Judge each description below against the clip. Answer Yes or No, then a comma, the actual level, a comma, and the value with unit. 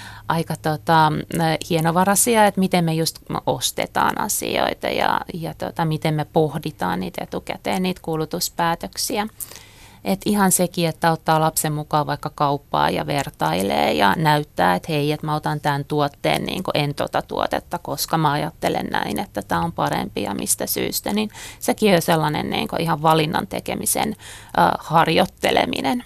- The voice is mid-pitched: Yes, medium, 155 Hz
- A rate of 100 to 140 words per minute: No, average, 150 wpm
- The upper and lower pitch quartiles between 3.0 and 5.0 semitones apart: No, narrow, 2.5 semitones